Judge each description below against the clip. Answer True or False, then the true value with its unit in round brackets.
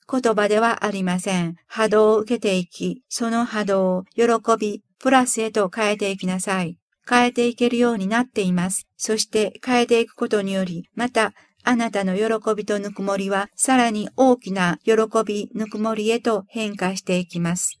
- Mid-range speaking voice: False (215 Hz)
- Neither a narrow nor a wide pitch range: True (3.0 semitones)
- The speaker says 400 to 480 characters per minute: False (340 characters per minute)